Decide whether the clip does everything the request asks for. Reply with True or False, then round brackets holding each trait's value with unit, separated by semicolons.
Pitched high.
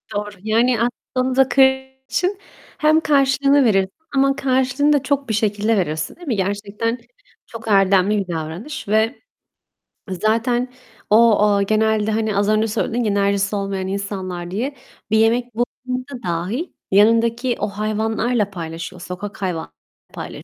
True (220 Hz)